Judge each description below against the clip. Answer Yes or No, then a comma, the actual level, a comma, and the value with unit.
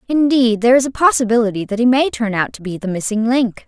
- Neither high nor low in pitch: No, high, 235 Hz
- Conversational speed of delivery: No, fast, 245 wpm